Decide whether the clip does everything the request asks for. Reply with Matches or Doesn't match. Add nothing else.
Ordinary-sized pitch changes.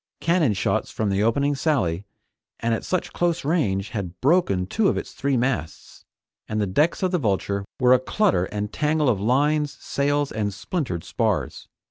Doesn't match